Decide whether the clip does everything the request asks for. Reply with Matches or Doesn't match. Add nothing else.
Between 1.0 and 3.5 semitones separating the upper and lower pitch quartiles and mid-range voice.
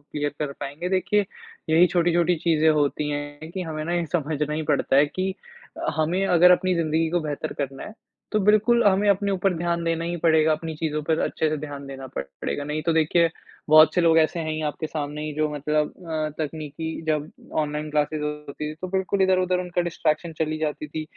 Matches